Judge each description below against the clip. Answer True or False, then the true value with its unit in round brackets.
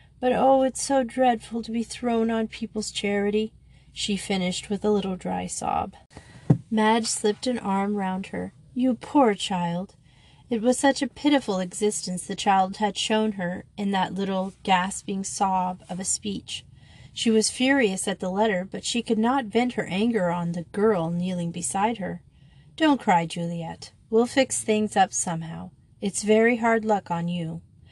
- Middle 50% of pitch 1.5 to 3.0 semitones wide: False (4.0 semitones)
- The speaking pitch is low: False (205 Hz)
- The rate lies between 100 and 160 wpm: False (170 wpm)